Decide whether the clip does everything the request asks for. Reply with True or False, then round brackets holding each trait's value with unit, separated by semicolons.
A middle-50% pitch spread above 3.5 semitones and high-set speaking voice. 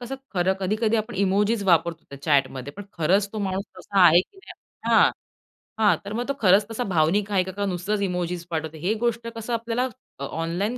True (4.1 semitones; 195 Hz)